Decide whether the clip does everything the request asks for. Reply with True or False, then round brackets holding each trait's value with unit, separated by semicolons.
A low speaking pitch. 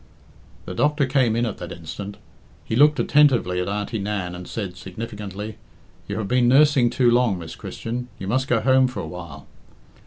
True (110 Hz)